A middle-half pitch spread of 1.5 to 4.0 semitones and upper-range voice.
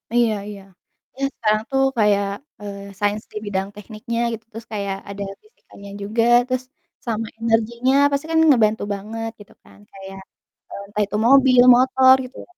Yes: average, 3.4 semitones; high, 220 Hz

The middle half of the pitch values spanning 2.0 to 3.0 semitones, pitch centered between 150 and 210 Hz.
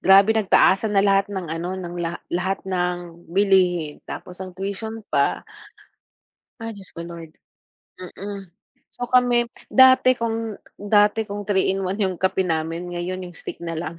Yes: average, 2.7 semitones; high, 190 Hz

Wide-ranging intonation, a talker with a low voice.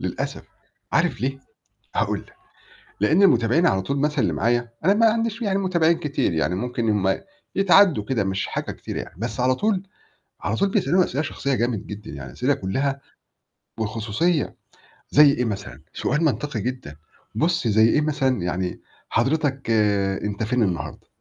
Yes: wide, 7.0 semitones; low, 130 Hz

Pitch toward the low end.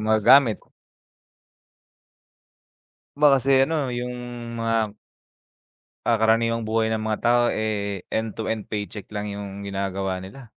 Yes: low, 110 Hz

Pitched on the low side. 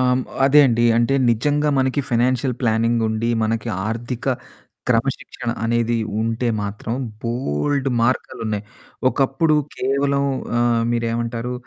Yes: low, 120 Hz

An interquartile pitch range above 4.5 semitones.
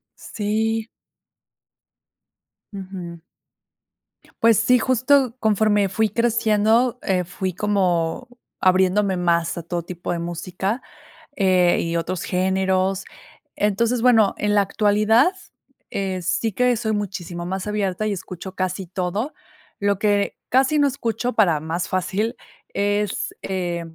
No: average, 3.3 semitones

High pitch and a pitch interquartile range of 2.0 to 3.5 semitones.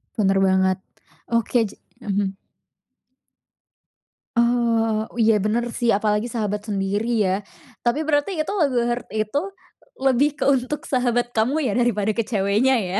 Yes: high, 225 Hz; average, 3.1 semitones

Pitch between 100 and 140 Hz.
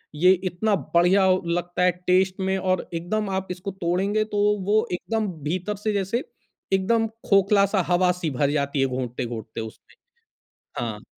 No: medium, 185 Hz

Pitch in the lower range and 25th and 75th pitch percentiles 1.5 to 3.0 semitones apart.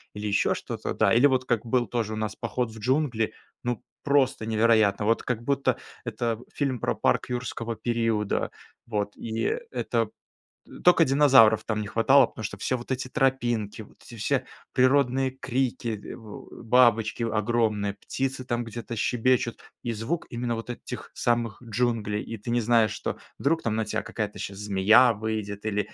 Yes: low, 115 Hz; average, 2.7 semitones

